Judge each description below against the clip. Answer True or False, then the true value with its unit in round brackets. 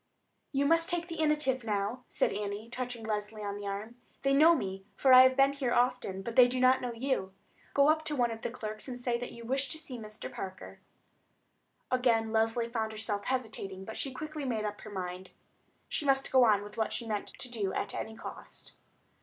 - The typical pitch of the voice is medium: False (235 Hz)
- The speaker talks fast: True (220 wpm)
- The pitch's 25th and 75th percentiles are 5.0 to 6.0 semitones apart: False (3.7 semitones)